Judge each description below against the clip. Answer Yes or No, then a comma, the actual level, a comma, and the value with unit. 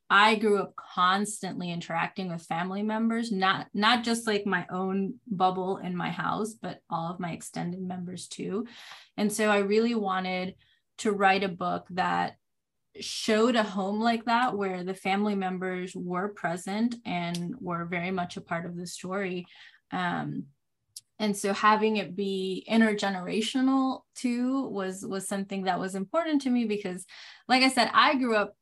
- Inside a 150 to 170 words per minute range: Yes, average, 165 wpm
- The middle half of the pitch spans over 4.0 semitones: No, average, 3.2 semitones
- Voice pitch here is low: No, high, 195 Hz